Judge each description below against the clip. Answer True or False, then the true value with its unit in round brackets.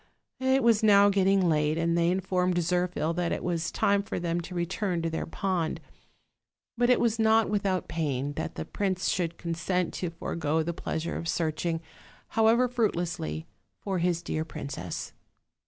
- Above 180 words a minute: False (170 wpm)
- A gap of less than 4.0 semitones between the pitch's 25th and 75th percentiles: True (3.3 semitones)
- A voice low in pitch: False (175 Hz)